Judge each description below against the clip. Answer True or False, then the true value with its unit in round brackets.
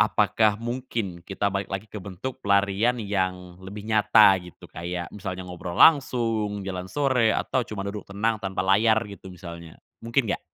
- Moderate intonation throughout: True (3.1 semitones)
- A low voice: True (100 Hz)